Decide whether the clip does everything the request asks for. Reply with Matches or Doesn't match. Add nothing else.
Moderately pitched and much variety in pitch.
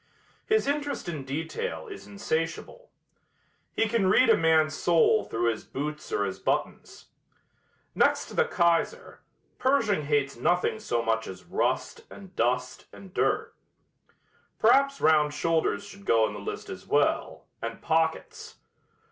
Matches